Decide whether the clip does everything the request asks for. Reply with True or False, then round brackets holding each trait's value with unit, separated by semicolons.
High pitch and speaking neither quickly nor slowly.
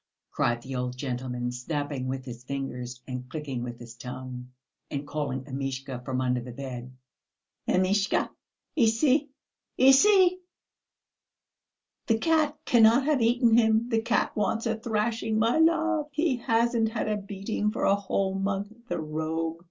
True (195 Hz; 145 wpm)